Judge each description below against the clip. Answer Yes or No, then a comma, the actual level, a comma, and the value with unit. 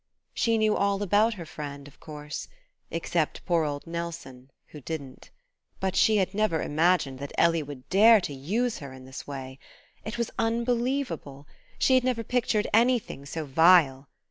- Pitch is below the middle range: No, medium, 170 Hz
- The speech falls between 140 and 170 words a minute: Yes, average, 165 wpm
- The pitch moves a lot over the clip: Yes, wide, 7.4 semitones